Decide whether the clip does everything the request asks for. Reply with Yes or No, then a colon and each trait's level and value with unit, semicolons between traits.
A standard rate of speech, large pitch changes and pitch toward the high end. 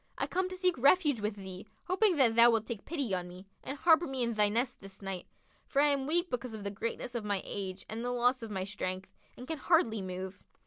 No: fast, 250 wpm; wide, 6.1 semitones; high, 230 Hz